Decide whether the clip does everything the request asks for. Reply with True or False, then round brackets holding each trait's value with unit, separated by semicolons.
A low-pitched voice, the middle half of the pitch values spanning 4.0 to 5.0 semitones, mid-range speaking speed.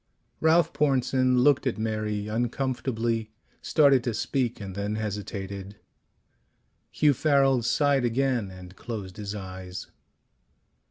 False (115 Hz; 4.5 semitones; 110 wpm)